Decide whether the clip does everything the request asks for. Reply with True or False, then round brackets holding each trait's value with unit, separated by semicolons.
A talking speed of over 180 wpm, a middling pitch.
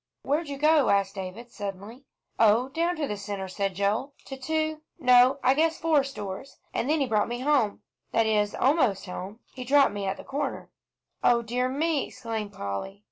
False (190 wpm; 245 Hz)